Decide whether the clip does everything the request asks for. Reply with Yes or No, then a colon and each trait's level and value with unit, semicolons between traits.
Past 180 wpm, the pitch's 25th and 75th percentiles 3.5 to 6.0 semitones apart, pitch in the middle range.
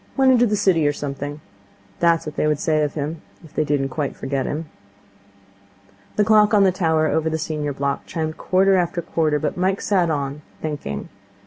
Yes: average, 200 wpm; average, 3.9 semitones; medium, 155 Hz